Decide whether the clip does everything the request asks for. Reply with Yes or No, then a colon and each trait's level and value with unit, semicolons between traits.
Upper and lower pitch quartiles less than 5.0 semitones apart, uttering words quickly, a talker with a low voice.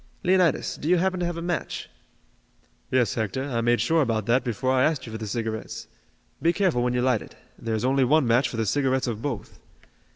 No: average, 5.3 semitones; fast, 225 wpm; low, 130 Hz